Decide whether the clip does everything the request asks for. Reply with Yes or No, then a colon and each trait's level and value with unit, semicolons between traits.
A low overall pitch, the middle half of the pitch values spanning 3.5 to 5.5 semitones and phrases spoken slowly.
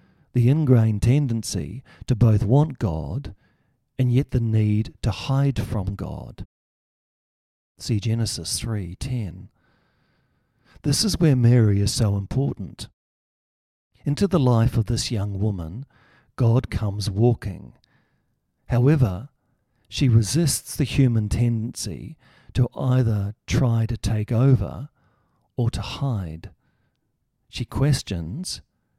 Yes: low, 115 Hz; average, 3.8 semitones; slow, 110 wpm